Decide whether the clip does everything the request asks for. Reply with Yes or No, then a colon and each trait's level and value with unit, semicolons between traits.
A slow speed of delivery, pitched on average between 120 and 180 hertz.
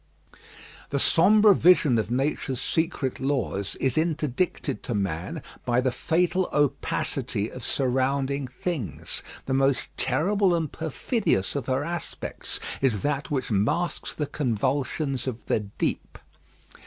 Yes: slow, 130 wpm; low, 135 Hz